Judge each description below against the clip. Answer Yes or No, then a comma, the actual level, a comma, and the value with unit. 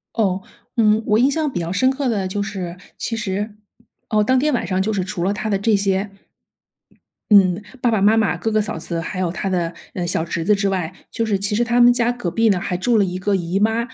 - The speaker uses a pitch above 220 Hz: No, high, 205 Hz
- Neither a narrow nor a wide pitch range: Yes, average, 3.3 semitones